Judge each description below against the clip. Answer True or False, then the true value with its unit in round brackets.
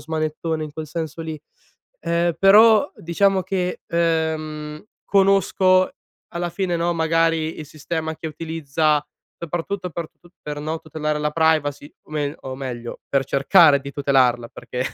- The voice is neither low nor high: True (160 Hz)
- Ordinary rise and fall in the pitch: False (2.3 semitones)